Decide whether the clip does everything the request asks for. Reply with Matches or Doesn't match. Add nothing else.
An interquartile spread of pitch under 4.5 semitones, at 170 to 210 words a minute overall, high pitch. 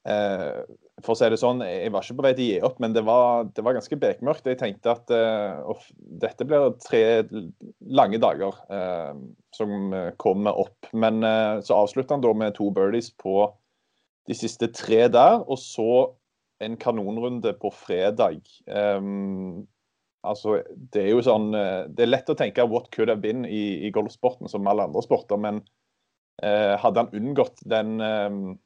Doesn't match